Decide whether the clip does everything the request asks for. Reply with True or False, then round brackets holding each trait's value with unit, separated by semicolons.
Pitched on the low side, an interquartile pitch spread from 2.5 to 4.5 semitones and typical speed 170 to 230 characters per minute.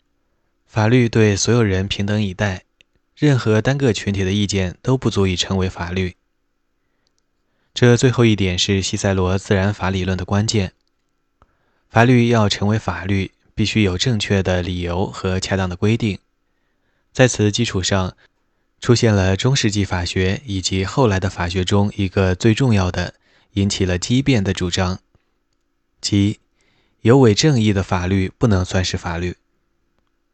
True (100 Hz; 2.8 semitones; 225 characters per minute)